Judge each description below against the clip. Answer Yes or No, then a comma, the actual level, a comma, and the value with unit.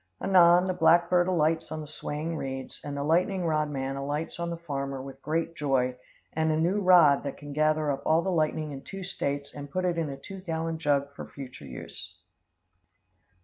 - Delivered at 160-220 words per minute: Yes, fast, 205 wpm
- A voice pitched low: No, medium, 155 Hz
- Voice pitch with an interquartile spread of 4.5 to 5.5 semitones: No, average, 3.3 semitones